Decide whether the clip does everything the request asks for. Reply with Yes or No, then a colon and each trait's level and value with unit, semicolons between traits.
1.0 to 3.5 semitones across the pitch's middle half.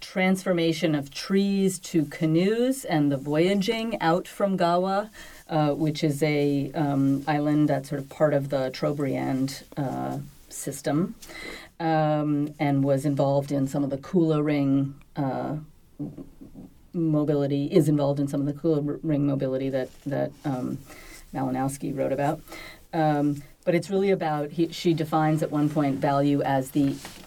Yes: average, 2.8 semitones